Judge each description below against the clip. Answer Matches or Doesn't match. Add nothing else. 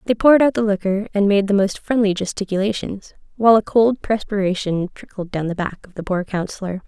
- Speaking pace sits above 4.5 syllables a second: Matches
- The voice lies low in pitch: Doesn't match